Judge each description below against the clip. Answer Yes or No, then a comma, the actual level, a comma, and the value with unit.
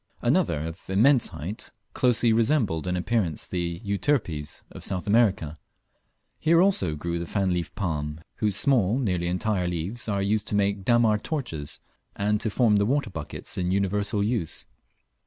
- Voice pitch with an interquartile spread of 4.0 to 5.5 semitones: Yes, average, 4.6 semitones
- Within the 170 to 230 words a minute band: No, average, 160 wpm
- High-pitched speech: No, low, 100 Hz